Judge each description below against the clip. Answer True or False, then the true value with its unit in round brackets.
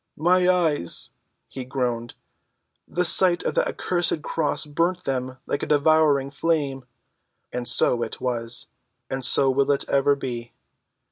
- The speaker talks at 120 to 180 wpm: True (140 wpm)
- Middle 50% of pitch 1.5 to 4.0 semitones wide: False (4.4 semitones)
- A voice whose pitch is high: False (140 Hz)